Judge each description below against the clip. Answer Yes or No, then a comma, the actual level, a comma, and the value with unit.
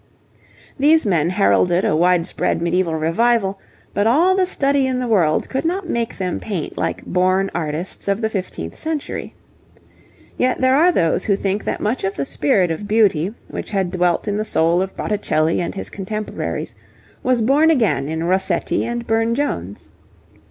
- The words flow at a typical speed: Yes, average, 170 wpm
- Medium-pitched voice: No, high, 195 Hz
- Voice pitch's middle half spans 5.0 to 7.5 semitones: Yes, wide, 5.6 semitones